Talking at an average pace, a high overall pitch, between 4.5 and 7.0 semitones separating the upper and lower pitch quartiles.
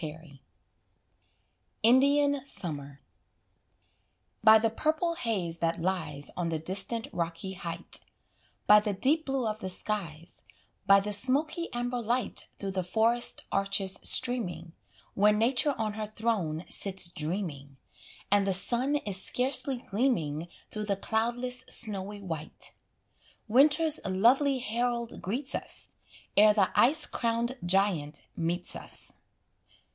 No: slow, 125 wpm; high, 210 Hz; wide, 5.5 semitones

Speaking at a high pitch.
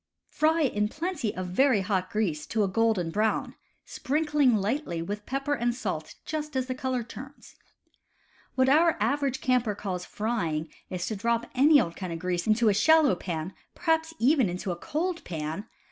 Yes: high, 230 Hz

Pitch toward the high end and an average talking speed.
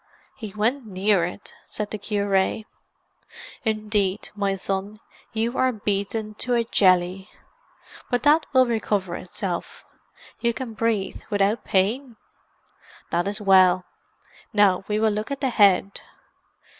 No: high, 210 Hz; slow, 130 wpm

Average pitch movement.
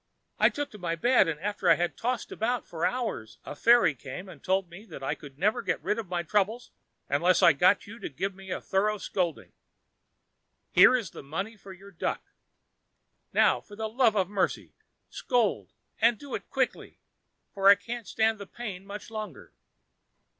Yes: average, 4.0 semitones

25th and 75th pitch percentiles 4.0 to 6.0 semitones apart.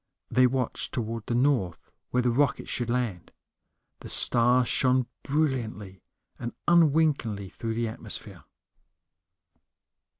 No: average, 2.9 semitones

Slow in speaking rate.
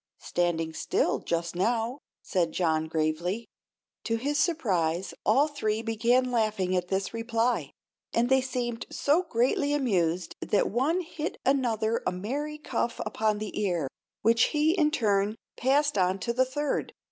No: average, 145 wpm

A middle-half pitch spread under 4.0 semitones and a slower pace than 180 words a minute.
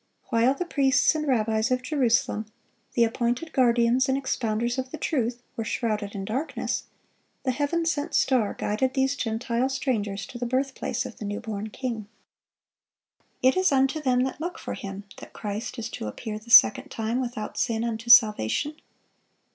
Yes: average, 3.2 semitones; average, 170 wpm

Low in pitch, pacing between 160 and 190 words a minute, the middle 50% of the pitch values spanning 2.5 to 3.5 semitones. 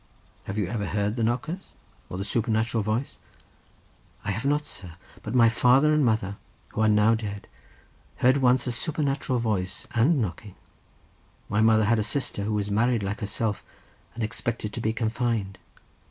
Yes: low, 110 Hz; average, 170 wpm; average, 2.9 semitones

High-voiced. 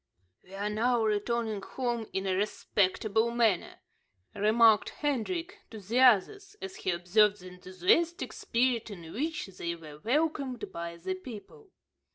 Yes: high, 220 Hz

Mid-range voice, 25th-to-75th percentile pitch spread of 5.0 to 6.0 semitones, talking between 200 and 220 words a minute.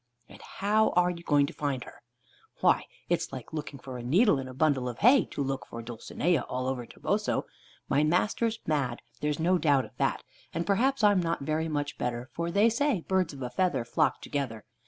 Yes: medium, 150 Hz; wide, 5.6 semitones; fast, 205 wpm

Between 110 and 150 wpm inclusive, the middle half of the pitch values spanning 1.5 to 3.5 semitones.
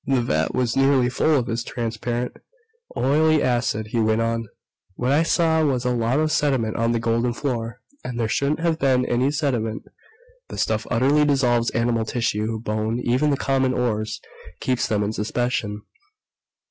No: average, 170 wpm; average, 2.9 semitones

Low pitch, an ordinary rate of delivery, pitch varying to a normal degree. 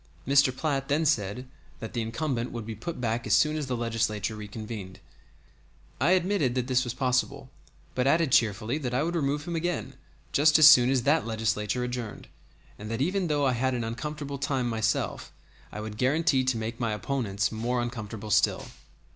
Yes: low, 125 Hz; average, 185 wpm; average, 4.2 semitones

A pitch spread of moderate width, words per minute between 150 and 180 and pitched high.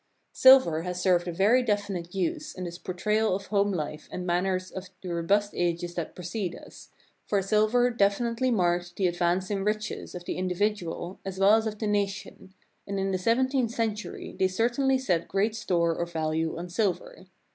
No: average, 3.5 semitones; average, 190 wpm; high, 195 Hz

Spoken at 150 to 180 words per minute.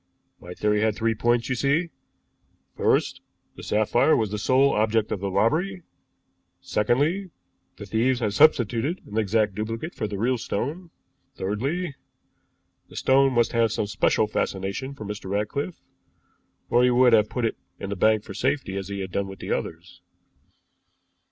Yes: average, 160 wpm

